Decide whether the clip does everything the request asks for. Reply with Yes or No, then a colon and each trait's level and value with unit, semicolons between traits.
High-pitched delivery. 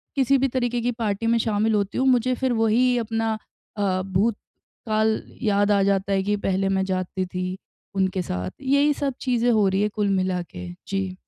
Yes: high, 210 Hz